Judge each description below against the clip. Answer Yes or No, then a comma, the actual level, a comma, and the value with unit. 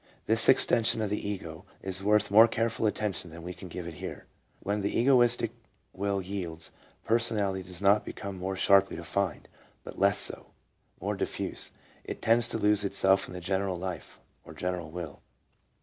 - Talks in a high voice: No, low, 100 Hz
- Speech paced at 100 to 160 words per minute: No, average, 170 wpm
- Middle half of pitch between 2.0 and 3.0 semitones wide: Yes, average, 2.7 semitones